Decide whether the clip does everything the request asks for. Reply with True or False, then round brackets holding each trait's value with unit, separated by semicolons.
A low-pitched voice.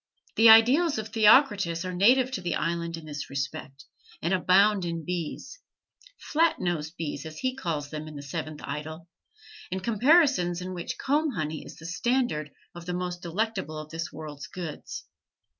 False (175 Hz)